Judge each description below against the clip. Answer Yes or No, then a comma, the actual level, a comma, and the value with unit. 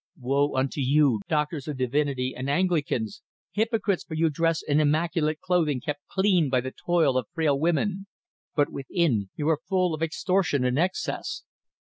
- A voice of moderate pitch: Yes, medium, 150 Hz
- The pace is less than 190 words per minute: Yes, average, 160 wpm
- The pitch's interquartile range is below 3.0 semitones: No, average, 4.0 semitones